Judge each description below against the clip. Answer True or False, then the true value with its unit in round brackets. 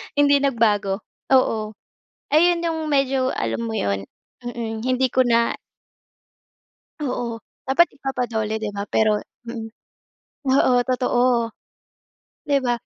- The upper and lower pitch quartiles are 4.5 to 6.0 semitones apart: False (3.4 semitones)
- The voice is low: False (245 Hz)